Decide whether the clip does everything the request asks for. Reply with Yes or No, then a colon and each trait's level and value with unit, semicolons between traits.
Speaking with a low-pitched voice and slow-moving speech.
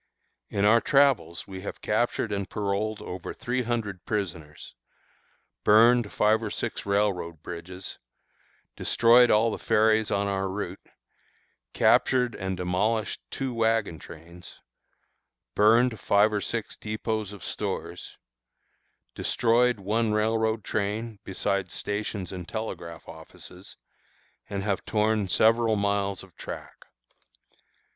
Yes: low, 105 Hz; slow, 115 wpm